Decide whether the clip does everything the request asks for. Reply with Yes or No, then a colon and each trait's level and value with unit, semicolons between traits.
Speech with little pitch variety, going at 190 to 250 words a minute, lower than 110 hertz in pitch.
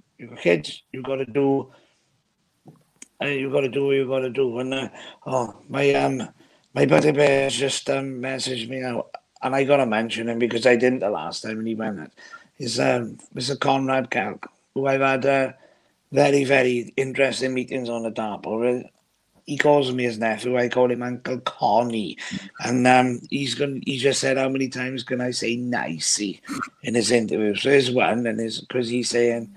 No: narrow, 2.2 semitones; average, 195 wpm; low, 125 Hz